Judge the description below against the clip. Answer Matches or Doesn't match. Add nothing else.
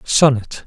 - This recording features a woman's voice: Doesn't match